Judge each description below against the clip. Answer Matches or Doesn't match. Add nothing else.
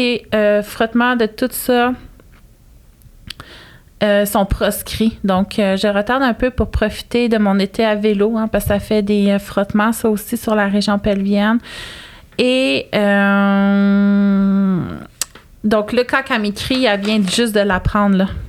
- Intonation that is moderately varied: Doesn't match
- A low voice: Doesn't match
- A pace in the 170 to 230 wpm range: Doesn't match